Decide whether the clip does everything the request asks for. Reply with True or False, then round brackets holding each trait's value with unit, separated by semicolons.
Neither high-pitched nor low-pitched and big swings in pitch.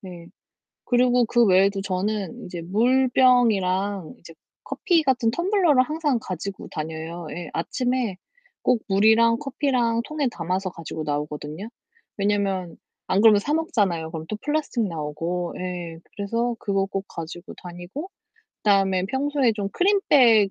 False (205 Hz; 5.7 semitones)